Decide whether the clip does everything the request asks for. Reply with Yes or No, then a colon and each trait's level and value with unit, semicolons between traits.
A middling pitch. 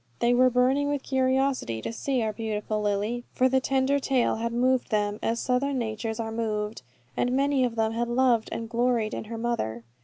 No: high, 235 Hz